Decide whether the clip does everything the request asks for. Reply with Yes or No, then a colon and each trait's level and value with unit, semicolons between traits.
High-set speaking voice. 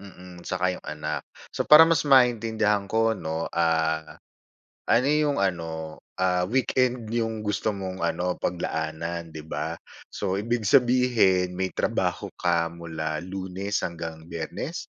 No: very low, 95 Hz